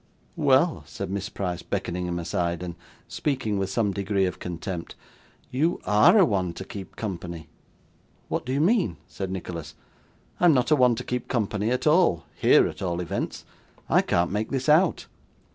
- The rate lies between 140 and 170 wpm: No, average, 180 wpm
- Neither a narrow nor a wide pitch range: No, wide, 6.1 semitones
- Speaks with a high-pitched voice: No, low, 100 Hz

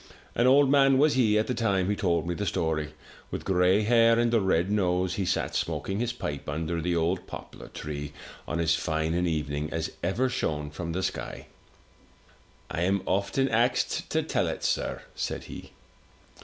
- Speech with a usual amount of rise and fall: No, wide, 5.9 semitones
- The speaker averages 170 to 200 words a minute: Yes, average, 185 wpm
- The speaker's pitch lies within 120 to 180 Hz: No, very low, 95 Hz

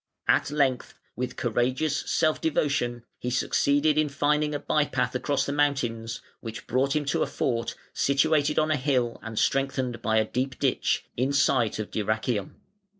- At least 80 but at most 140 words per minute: No, average, 165 wpm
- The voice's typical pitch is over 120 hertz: Yes, low, 135 Hz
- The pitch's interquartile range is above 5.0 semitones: No, average, 3.3 semitones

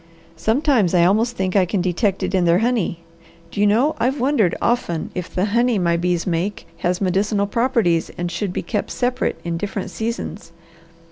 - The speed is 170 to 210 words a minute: Yes, average, 185 wpm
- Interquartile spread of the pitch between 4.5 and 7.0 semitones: Yes, average, 4.8 semitones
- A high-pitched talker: Yes, high, 200 Hz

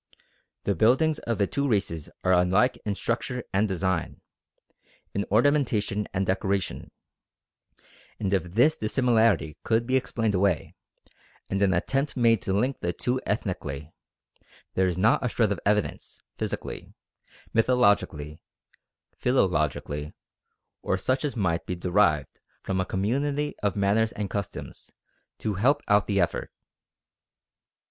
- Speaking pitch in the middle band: No, low, 105 Hz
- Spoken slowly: Yes, slow, 130 wpm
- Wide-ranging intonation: No, average, 4.4 semitones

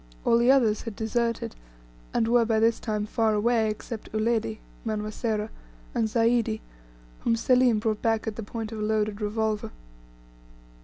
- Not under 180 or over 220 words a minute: No, average, 160 wpm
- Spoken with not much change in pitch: Yes, narrow, 1.4 semitones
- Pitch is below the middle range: No, high, 220 Hz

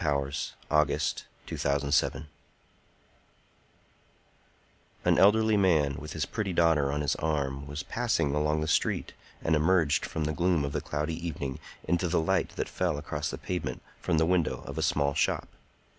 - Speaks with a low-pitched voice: Yes, very low, 75 Hz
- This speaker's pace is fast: No, average, 165 wpm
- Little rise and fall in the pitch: No, average, 3.1 semitones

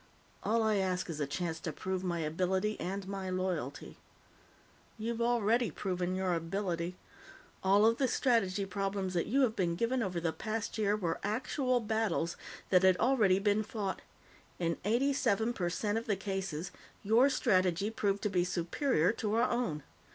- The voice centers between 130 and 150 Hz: No, high, 195 Hz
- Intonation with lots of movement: No, average, 3.7 semitones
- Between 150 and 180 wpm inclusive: Yes, average, 170 wpm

